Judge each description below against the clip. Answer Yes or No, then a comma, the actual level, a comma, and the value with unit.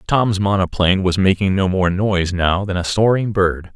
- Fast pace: No, average, 190 wpm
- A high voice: No, very low, 95 Hz